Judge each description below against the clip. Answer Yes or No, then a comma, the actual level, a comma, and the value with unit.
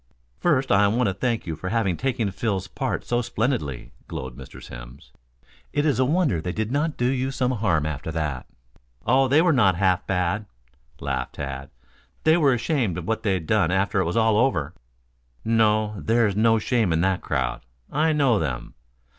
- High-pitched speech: No, low, 110 Hz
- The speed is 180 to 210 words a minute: Yes, average, 185 wpm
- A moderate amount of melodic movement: No, wide, 6.1 semitones